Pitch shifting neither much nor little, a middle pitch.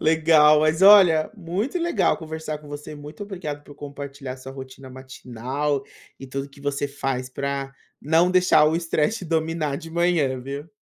Yes: average, 3.1 semitones; medium, 150 Hz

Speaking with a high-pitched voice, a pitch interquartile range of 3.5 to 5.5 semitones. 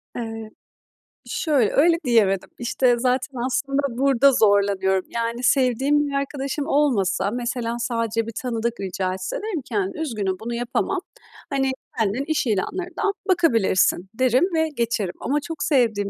Yes: high, 240 Hz; average, 4.3 semitones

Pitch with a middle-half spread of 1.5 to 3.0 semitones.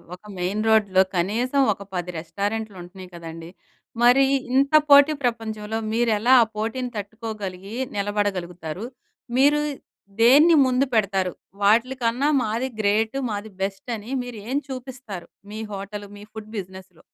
No: average, 4.1 semitones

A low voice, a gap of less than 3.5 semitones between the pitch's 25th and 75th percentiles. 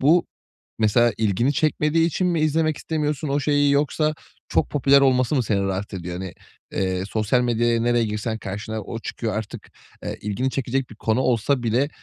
No: low, 125 Hz; average, 4.9 semitones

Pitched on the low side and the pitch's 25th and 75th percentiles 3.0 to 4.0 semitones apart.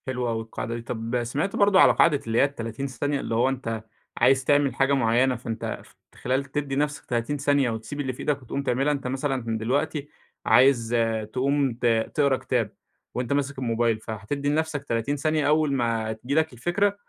Yes: low, 130 Hz; average, 3.6 semitones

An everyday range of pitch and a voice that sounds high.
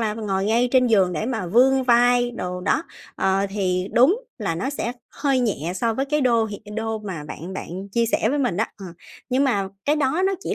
Yes: average, 4.8 semitones; high, 225 Hz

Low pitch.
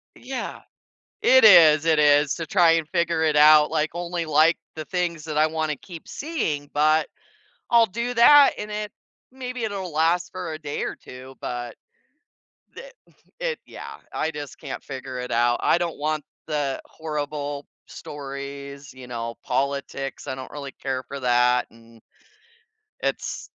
No: medium, 155 Hz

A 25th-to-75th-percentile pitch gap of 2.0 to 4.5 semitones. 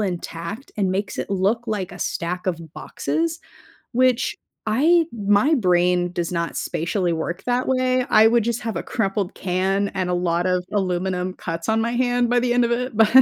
No: average, 5.0 semitones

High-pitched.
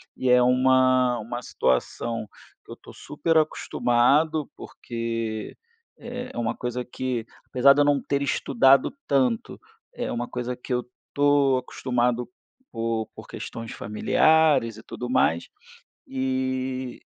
No: low, 125 Hz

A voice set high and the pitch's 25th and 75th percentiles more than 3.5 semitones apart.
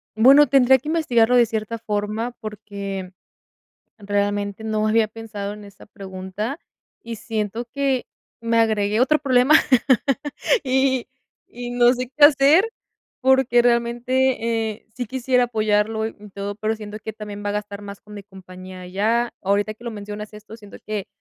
No: high, 220 Hz; average, 3.1 semitones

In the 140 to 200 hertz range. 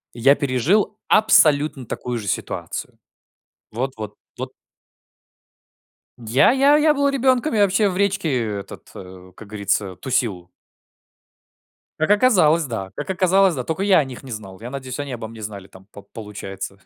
No: low, 130 Hz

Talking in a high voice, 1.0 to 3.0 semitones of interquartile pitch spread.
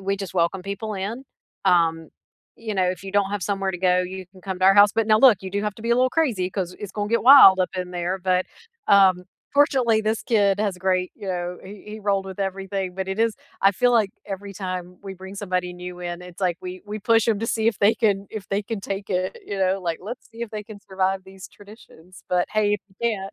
Yes: high, 195 Hz; narrow, 2.4 semitones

